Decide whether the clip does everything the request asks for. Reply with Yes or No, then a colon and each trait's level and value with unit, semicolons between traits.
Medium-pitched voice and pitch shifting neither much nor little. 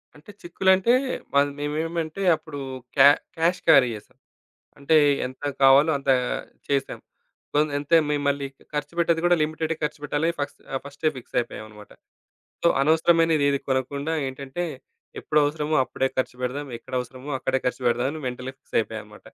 Yes: medium, 145 Hz; average, 3.3 semitones